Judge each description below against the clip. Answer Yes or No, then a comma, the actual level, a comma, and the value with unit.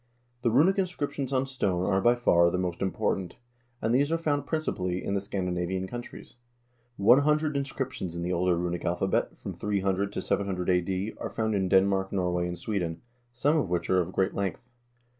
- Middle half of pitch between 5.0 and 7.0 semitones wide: Yes, wide, 5.6 semitones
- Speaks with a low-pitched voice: Yes, very low, 95 Hz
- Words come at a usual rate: Yes, average, 185 wpm